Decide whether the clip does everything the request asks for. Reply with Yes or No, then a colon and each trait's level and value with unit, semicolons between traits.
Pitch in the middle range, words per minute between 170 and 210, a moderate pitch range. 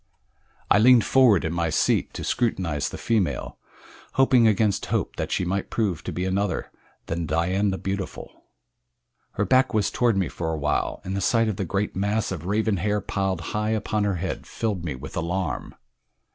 No: low, 100 Hz; average, 185 wpm; average, 3.9 semitones